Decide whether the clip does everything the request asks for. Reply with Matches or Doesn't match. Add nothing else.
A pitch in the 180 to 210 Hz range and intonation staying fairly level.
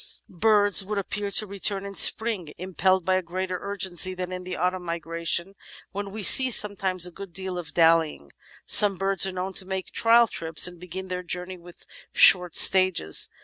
Matches